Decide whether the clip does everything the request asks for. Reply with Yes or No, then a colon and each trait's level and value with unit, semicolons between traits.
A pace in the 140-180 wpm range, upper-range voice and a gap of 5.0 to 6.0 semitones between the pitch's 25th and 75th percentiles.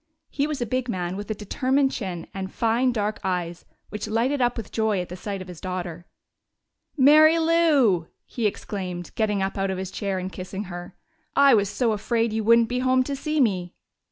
No: fast, 205 wpm; high, 215 Hz; average, 5.3 semitones